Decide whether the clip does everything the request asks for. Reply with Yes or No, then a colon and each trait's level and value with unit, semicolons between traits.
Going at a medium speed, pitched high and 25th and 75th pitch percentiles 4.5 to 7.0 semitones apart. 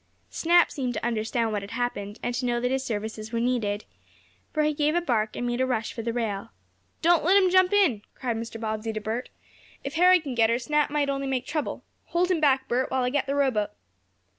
No: fast, 235 wpm; very high, 250 Hz; average, 4.8 semitones